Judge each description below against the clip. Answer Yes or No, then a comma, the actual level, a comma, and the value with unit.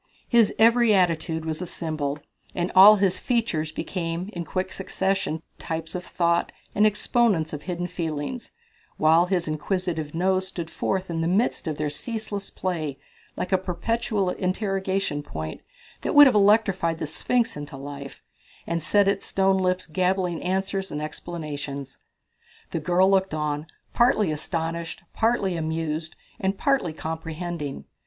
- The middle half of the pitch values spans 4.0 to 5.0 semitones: No, average, 3.5 semitones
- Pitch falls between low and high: Yes, medium, 175 Hz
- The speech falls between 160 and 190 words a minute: No, average, 145 wpm